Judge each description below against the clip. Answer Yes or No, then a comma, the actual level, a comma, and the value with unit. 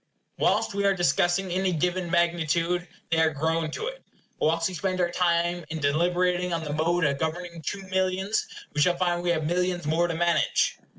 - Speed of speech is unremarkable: Yes, average, 190 wpm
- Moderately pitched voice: Yes, medium, 175 Hz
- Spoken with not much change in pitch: Yes, narrow, 1.8 semitones